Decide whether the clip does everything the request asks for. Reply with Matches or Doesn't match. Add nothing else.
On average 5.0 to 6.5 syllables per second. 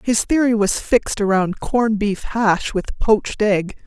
Doesn't match